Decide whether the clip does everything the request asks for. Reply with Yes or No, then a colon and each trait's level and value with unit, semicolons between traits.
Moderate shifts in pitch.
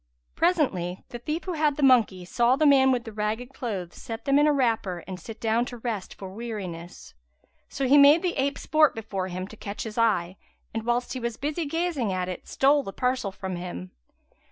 No: wide, 6.3 semitones